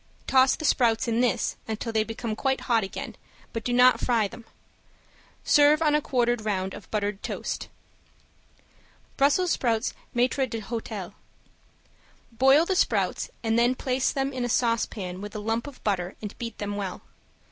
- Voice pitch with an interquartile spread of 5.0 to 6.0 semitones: No, average, 3.3 semitones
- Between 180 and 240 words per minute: No, average, 160 wpm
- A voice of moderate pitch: No, high, 230 Hz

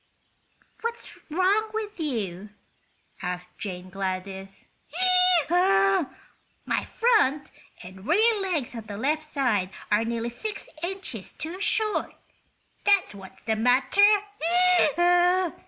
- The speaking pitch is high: Yes, very high, 295 Hz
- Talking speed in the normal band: No, slow, 100 wpm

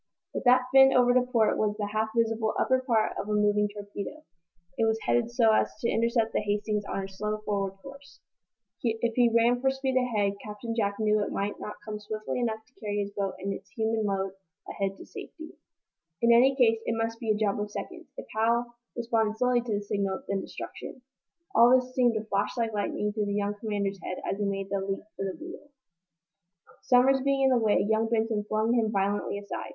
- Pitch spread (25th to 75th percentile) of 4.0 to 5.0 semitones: No, average, 2.7 semitones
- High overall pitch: Yes, high, 220 Hz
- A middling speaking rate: No, fast, 215 wpm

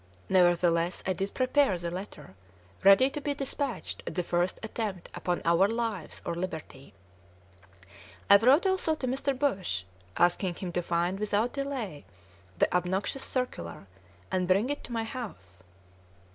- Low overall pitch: No, high, 195 Hz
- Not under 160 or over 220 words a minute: No, average, 145 wpm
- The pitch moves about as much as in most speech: No, wide, 6.4 semitones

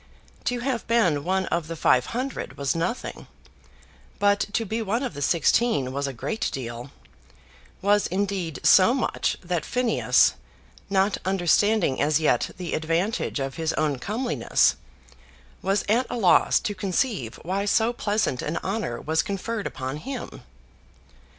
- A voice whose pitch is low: No, high, 190 Hz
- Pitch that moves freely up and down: Yes, wide, 6.2 semitones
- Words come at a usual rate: Yes, average, 145 wpm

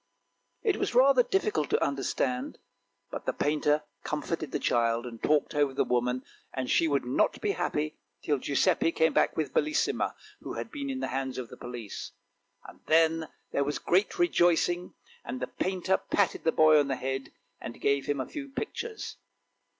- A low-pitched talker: No, medium, 150 Hz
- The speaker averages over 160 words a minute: Yes, average, 175 wpm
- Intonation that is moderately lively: No, wide, 5.7 semitones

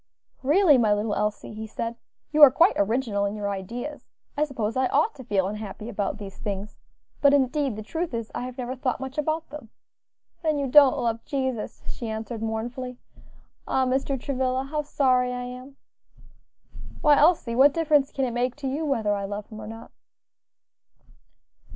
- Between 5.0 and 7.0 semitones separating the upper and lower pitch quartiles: No, average, 4.3 semitones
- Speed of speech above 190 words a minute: No, average, 180 wpm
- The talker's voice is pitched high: Yes, very high, 250 Hz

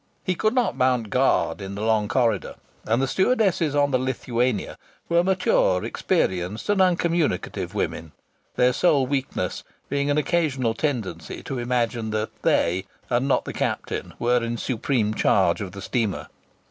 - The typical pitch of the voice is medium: No, low, 125 Hz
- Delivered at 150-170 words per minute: Yes, average, 155 wpm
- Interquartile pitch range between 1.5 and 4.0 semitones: No, average, 5.1 semitones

